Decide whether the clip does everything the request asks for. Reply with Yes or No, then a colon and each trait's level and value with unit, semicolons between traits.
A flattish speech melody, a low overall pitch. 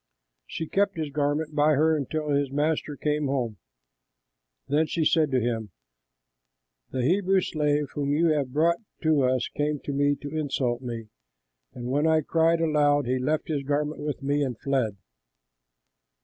No: narrow, 2.3 semitones; medium, 145 Hz